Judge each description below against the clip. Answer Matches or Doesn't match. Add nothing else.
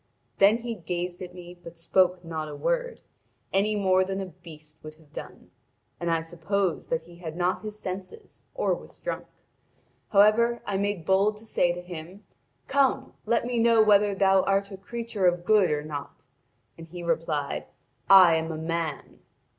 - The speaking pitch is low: Doesn't match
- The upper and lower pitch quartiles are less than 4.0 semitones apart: Matches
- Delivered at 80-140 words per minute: Doesn't match